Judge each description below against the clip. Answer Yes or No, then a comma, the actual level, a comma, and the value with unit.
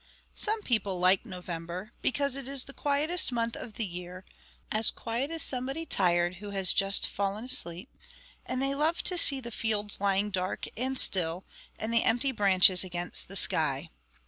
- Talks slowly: No, average, 170 wpm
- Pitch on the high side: Yes, high, 215 Hz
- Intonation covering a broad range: Yes, wide, 6.2 semitones